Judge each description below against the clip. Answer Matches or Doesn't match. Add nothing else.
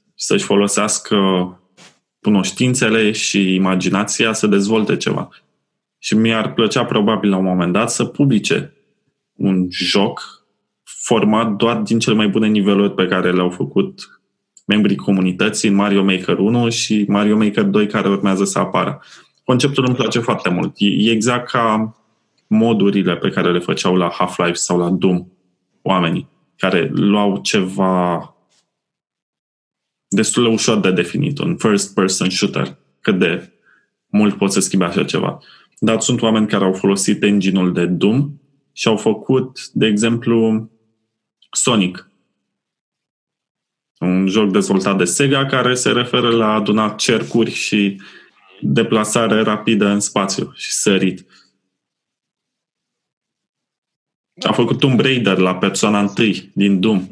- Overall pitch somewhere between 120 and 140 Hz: Doesn't match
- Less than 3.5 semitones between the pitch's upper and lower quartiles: Matches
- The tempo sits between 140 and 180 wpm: Doesn't match